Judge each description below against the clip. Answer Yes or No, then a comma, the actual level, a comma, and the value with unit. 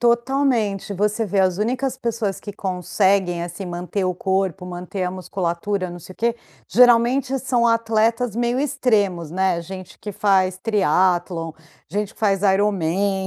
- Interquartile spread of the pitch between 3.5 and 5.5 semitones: Yes, average, 3.9 semitones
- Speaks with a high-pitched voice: Yes, high, 200 Hz